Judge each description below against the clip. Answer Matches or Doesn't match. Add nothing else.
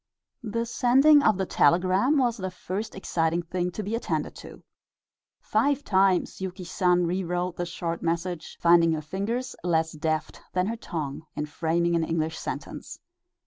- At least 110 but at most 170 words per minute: Matches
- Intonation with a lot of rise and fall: Doesn't match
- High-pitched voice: Doesn't match